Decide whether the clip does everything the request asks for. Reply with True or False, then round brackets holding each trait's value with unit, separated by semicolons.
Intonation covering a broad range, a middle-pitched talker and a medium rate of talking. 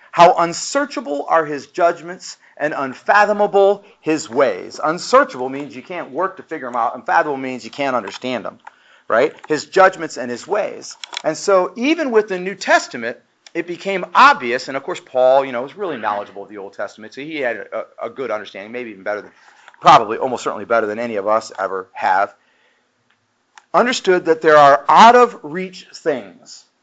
True (6.7 semitones; 160 Hz; 185 wpm)